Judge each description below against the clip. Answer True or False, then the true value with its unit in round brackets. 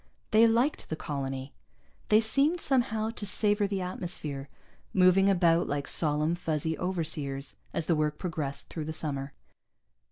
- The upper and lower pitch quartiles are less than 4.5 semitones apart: False (5.6 semitones)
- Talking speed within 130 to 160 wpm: True (140 wpm)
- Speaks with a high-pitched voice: False (170 Hz)